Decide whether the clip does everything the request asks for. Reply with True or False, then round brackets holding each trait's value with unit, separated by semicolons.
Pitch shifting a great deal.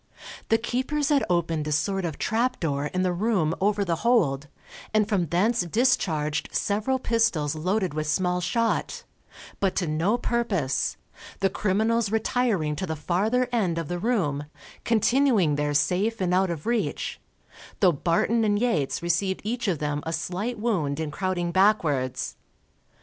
True (5.8 semitones)